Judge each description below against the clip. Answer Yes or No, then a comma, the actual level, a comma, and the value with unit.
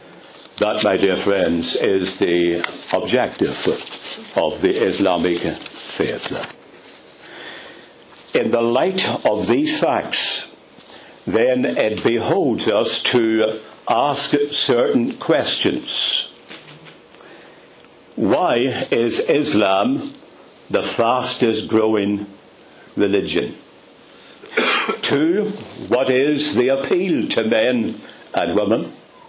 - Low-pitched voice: Yes, low, 115 Hz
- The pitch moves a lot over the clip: Yes, wide, 6.0 semitones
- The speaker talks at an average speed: No, slow, 85 wpm